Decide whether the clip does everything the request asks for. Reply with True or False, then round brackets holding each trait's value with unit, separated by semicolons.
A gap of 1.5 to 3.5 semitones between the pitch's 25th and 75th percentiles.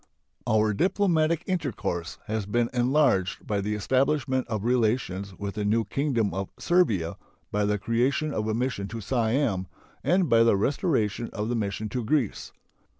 False (4.8 semitones)